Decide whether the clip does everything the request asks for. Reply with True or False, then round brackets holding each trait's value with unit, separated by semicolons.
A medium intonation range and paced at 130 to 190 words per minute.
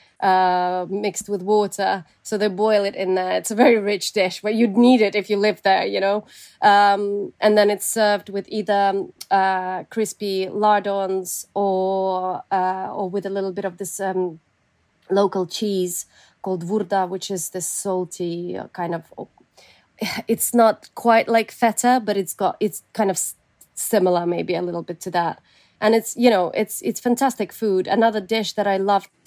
False (2.3 semitones; 180 wpm)